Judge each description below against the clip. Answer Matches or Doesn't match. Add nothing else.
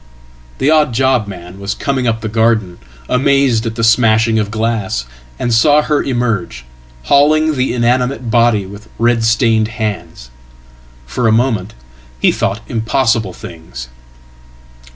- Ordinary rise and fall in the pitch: Matches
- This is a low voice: Matches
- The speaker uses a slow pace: Matches